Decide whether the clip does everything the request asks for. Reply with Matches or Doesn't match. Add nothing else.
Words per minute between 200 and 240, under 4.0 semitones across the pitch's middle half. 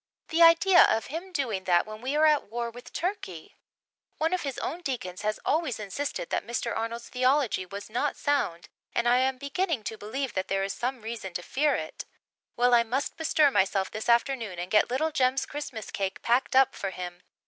Doesn't match